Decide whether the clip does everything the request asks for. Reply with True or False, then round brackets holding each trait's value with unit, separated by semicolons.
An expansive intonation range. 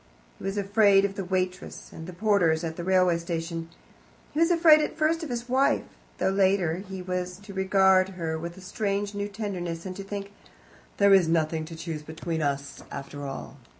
False (3.3 semitones)